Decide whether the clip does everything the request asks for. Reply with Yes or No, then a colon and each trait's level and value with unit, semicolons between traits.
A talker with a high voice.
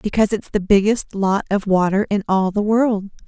Yes: high, 200 Hz